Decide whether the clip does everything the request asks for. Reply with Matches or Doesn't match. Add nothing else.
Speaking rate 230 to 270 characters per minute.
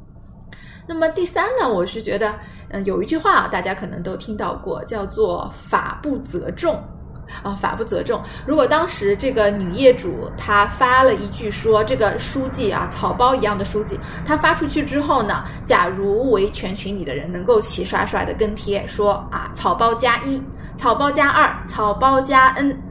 Matches